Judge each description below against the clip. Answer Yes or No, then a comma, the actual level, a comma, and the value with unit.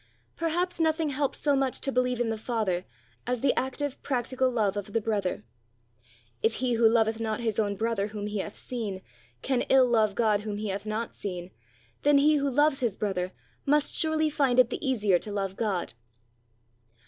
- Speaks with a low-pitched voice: No, high, 230 Hz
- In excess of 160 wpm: Yes, average, 185 wpm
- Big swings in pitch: No, average, 4.5 semitones